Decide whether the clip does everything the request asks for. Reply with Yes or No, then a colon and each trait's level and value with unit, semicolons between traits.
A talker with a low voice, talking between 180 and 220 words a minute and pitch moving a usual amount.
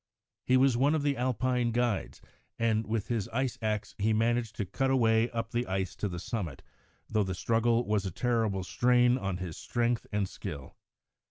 Yes: low, 115 Hz; average, 190 wpm; average, 3.0 semitones